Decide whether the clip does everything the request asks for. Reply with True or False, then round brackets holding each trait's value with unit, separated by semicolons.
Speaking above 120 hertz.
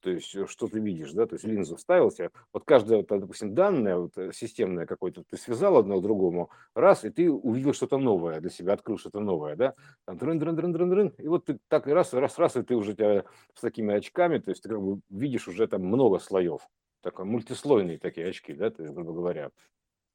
True (135 Hz)